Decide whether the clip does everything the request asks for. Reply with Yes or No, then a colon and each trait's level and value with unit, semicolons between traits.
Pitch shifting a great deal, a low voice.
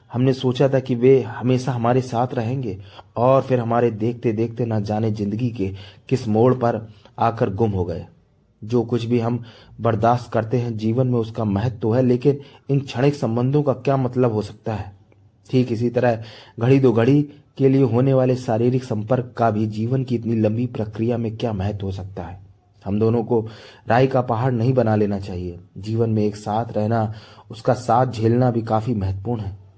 No: average, 2.8 semitones; low, 115 Hz